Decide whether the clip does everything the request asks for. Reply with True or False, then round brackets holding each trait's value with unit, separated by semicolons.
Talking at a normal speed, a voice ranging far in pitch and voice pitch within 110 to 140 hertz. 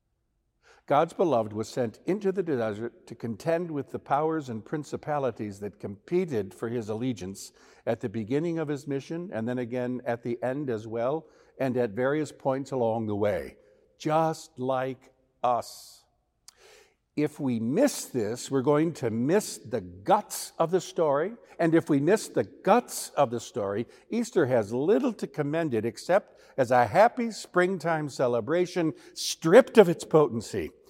True (155 wpm; 5.8 semitones; 135 Hz)